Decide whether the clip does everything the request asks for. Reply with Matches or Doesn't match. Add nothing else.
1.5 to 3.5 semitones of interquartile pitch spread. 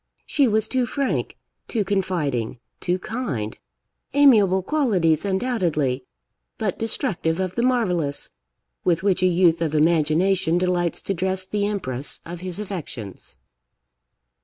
Doesn't match